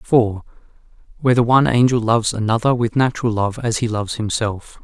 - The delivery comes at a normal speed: Yes, average, 160 wpm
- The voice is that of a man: Yes, male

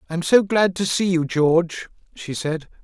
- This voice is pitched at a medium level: Yes, medium, 170 Hz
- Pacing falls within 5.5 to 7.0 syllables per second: No, 4.9 syllables/s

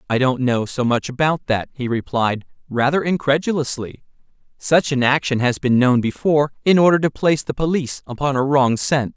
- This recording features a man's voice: Yes, male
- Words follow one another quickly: No, average, 185 wpm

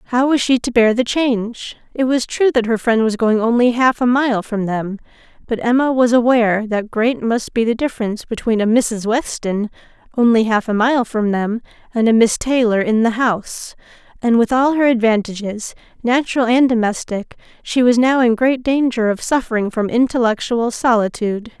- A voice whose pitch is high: Yes, high, 235 Hz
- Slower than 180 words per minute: No, average, 185 wpm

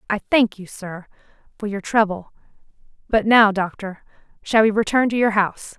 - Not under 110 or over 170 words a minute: Yes, average, 155 wpm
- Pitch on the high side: Yes, high, 210 Hz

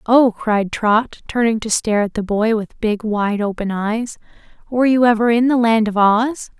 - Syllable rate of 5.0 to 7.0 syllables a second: No, 4.7 syllables/s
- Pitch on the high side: Yes, high, 220 Hz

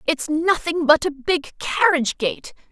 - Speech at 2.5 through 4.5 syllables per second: Yes, 4.3 syllables/s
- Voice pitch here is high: Yes, very high, 310 Hz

